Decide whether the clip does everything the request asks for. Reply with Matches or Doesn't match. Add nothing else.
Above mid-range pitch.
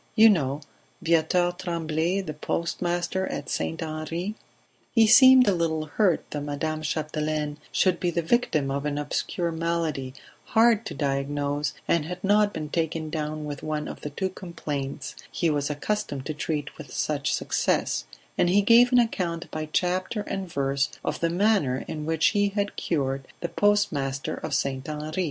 Doesn't match